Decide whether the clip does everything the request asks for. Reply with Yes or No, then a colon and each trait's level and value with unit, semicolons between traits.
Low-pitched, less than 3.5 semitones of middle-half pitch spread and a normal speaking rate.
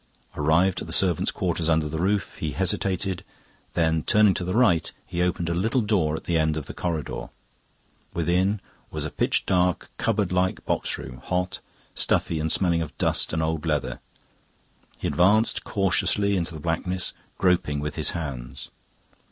Yes: very low, 85 Hz; average, 3.0 semitones; average, 165 wpm